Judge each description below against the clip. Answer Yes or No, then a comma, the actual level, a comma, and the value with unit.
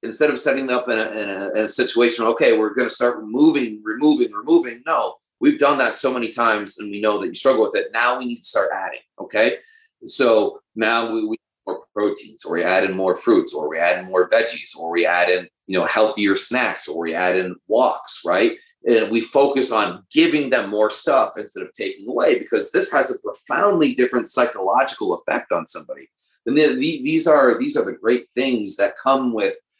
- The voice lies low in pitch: Yes, low, 125 Hz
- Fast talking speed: Yes, fast, 210 wpm